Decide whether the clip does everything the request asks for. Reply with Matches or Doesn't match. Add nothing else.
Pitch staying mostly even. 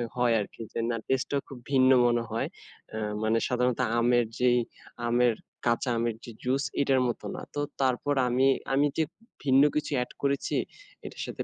Matches